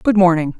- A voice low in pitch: No, medium, 180 Hz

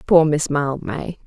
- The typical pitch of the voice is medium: Yes, medium, 150 Hz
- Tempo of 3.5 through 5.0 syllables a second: Yes, 3.7 syllables/s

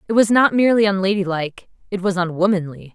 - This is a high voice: Yes, high, 195 Hz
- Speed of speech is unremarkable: Yes, average, 165 wpm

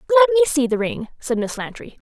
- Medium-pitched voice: No, very high, 290 Hz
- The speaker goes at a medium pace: No, fast, 230 wpm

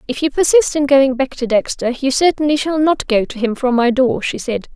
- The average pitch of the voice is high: Yes, very high, 265 Hz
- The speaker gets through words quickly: Yes, fast, 255 wpm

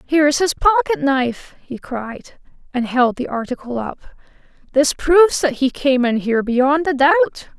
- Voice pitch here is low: No, very high, 275 Hz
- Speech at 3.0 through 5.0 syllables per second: Yes, 4.8 syllables/s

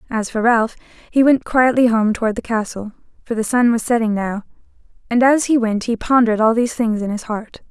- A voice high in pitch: Yes, high, 230 Hz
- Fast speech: Yes, fast, 220 wpm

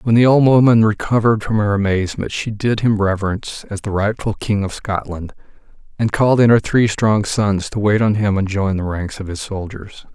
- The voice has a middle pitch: No, low, 105 Hz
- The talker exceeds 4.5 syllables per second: Yes, 5.4 syllables/s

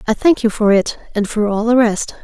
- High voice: Yes, high, 220 Hz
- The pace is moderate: No, fast, 240 wpm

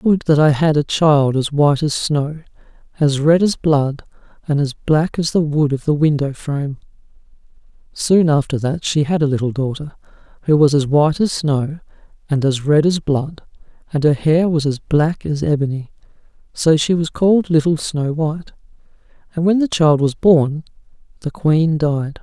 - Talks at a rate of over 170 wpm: Yes, average, 180 wpm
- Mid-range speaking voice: Yes, medium, 150 Hz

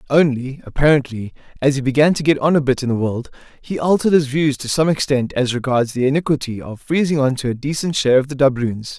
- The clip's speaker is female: No, male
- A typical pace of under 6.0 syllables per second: No, 6.1 syllables/s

